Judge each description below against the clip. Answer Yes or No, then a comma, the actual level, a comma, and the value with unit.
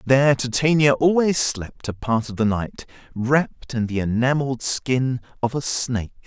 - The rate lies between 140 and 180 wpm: Yes, average, 165 wpm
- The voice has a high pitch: No, low, 125 Hz